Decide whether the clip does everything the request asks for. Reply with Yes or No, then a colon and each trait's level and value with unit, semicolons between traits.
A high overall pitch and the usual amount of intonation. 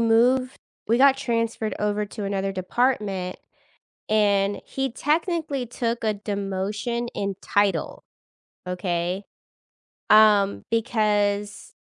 Yes: high, 210 Hz; average, 3.2 semitones